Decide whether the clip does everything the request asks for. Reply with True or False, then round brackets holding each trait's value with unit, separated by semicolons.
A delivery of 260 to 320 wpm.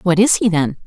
True (280 wpm)